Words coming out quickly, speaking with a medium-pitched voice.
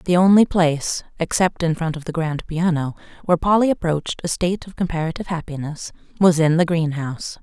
No: average, 180 wpm; medium, 165 Hz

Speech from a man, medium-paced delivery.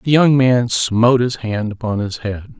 No: male; fast, 210 wpm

